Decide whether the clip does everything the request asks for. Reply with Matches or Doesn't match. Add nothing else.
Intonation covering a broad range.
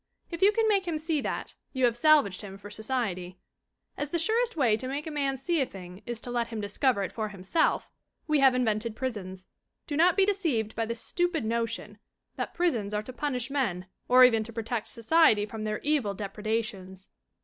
Matches